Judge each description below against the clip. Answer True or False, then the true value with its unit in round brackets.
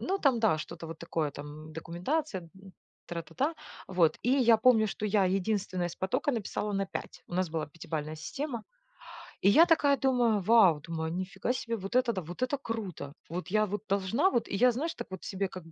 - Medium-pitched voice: False (195 Hz)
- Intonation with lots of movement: True (6.2 semitones)